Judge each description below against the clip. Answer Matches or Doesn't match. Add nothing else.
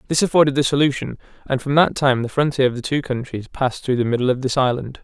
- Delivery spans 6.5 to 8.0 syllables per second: Matches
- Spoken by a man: Matches